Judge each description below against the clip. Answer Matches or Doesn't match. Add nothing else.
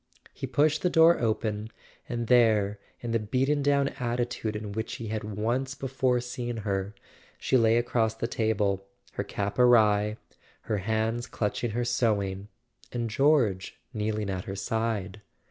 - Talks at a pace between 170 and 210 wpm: Doesn't match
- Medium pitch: Doesn't match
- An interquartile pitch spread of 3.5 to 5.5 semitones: Doesn't match